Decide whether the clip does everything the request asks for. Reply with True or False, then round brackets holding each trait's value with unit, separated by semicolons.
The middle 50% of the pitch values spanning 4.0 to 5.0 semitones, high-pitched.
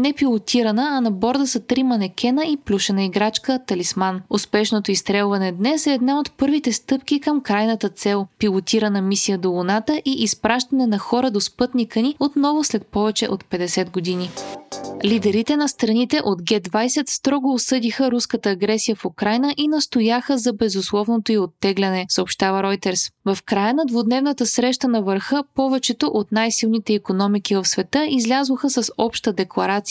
True (4.6 semitones; 225 Hz)